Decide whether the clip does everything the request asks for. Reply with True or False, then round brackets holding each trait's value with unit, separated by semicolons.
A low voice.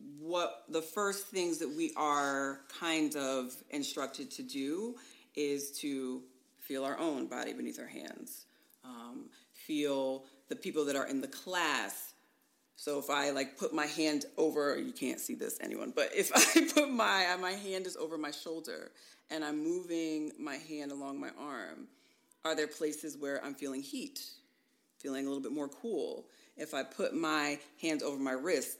False (155 Hz)